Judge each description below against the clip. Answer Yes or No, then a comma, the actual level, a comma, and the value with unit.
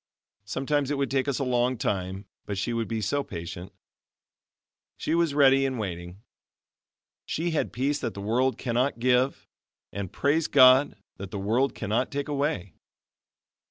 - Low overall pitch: Yes, low, 125 Hz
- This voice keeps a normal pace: Yes, average, 160 wpm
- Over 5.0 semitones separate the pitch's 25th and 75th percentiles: Yes, wide, 5.4 semitones